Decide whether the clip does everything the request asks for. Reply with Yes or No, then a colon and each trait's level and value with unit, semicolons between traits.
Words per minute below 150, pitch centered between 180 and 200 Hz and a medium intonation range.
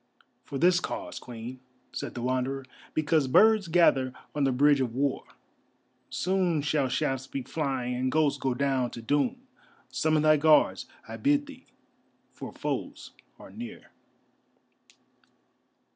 No: slow, 135 wpm; medium, 145 Hz; average, 4.7 semitones